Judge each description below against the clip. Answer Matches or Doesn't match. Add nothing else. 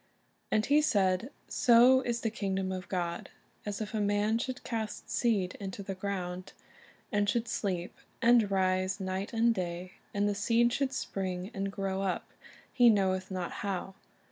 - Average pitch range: Matches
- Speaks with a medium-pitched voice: Doesn't match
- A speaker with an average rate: Matches